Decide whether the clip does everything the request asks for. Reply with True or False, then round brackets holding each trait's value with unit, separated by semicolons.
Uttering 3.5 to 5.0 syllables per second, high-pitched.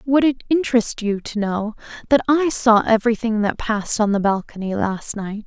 False (5.2 syllables/s; 225 Hz)